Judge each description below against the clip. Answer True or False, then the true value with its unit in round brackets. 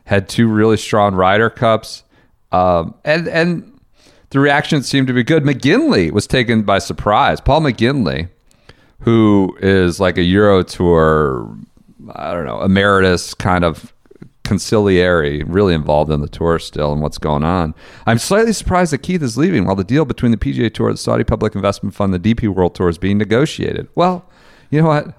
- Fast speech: False (180 wpm)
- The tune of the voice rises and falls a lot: True (6.1 semitones)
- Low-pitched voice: True (105 Hz)